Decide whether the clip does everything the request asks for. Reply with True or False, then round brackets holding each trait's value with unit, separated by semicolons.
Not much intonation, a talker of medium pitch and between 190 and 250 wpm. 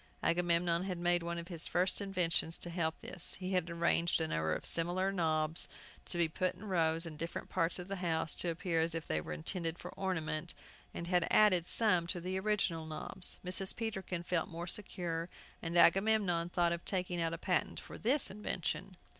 True (1.9 semitones; 175 Hz; 195 wpm)